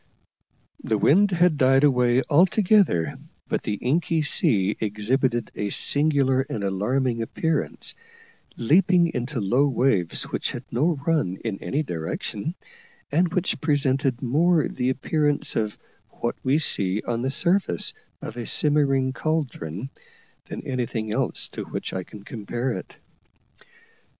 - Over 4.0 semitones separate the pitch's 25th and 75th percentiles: Yes, average, 5.3 semitones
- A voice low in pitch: Yes, low, 130 Hz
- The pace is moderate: No, slow, 130 wpm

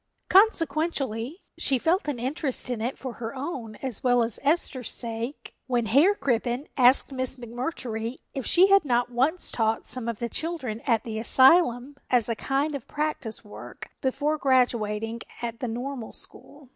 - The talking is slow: No, average, 165 wpm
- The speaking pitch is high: Yes, very high, 255 Hz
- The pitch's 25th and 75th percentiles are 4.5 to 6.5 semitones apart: No, average, 3.7 semitones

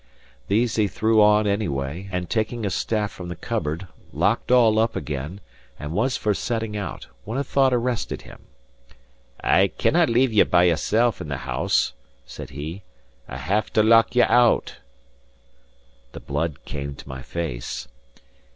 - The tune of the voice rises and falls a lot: Yes, wide, 6.2 semitones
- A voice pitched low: Yes, low, 105 Hz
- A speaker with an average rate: Yes, average, 160 wpm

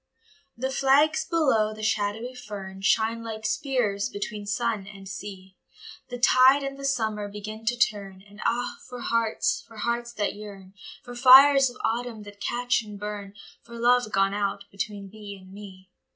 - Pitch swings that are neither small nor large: Yes, average, 3.3 semitones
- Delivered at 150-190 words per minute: Yes, average, 165 wpm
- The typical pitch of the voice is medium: No, high, 215 Hz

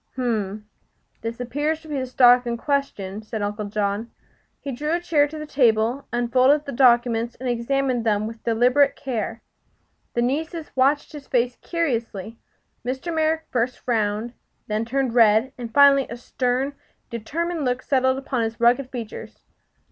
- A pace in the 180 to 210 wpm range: No, average, 160 wpm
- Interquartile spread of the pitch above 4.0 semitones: No, average, 3.4 semitones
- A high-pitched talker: Yes, high, 245 Hz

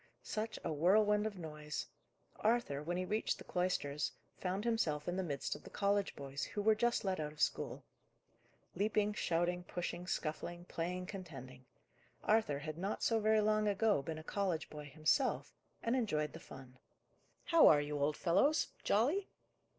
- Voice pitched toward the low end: No, medium, 180 Hz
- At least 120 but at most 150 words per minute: No, average, 165 wpm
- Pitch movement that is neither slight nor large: No, wide, 5.8 semitones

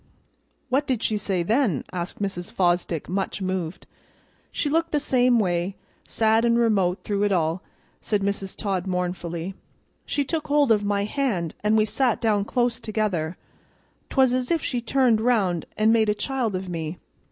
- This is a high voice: Yes, high, 210 Hz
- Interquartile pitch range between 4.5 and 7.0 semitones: Yes, average, 4.8 semitones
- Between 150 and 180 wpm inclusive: Yes, average, 170 wpm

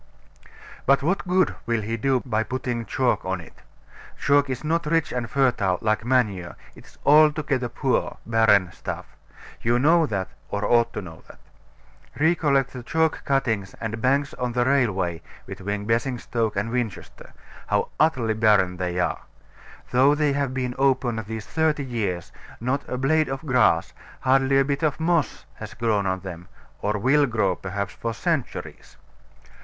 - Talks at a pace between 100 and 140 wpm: No, average, 160 wpm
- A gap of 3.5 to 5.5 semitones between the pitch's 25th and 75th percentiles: Yes, average, 4.6 semitones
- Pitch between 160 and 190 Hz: No, low, 125 Hz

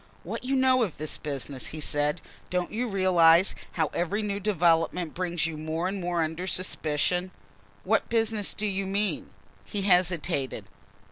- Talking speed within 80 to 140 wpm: No, average, 155 wpm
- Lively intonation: No, average, 3.7 semitones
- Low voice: No, medium, 180 Hz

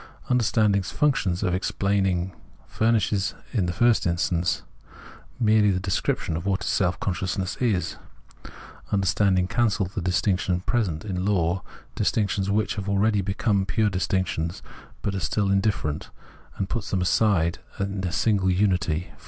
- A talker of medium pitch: No, very low, 95 Hz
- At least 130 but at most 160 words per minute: Yes, slow, 135 wpm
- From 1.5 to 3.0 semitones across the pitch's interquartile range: Yes, narrow, 2.4 semitones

